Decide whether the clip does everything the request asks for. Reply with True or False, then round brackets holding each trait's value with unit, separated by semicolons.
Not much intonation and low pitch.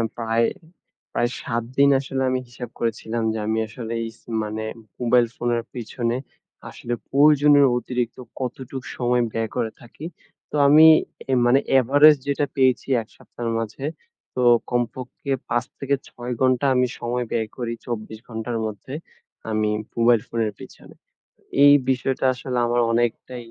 True (2.1 semitones; 120 Hz)